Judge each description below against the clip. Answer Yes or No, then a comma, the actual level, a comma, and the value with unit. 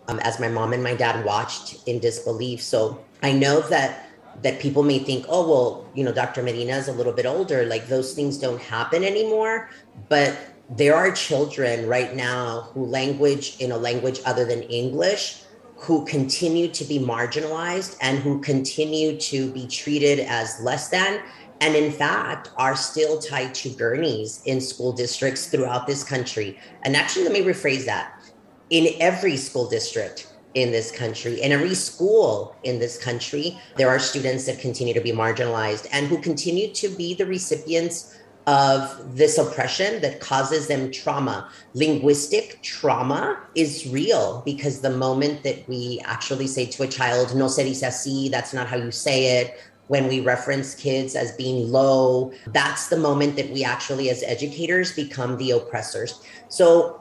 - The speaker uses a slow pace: No, average, 170 wpm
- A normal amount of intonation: Yes, average, 3.7 semitones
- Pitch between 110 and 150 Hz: Yes, low, 135 Hz